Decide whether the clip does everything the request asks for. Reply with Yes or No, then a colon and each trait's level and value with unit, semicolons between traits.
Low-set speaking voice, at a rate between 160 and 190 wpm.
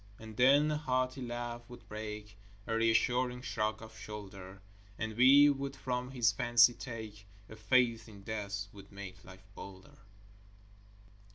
No: low, 115 Hz; average, 145 wpm